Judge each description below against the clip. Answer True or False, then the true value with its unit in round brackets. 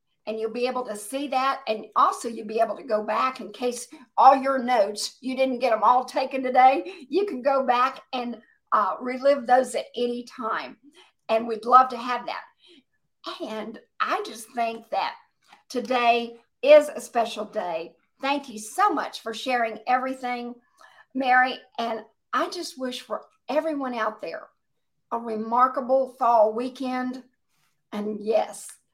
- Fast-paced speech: False (160 wpm)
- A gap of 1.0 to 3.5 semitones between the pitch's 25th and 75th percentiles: True (2.9 semitones)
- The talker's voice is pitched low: False (250 Hz)